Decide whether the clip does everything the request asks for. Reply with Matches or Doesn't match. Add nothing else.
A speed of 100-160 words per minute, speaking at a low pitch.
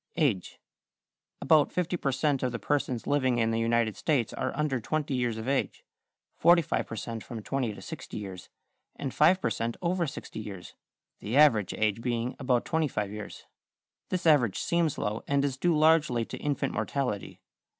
Doesn't match